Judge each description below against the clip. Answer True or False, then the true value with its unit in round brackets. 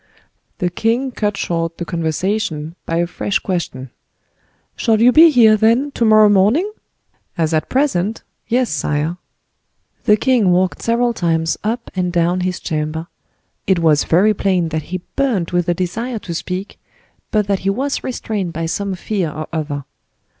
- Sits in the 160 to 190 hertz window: True (185 Hz)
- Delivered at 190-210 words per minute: False (160 wpm)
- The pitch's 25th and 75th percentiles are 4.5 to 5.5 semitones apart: True (4.9 semitones)